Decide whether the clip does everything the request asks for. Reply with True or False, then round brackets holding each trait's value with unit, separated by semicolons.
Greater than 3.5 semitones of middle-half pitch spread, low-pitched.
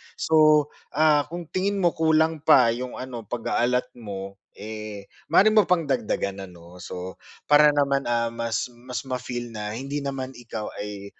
True (5.5 semitones; 125 Hz)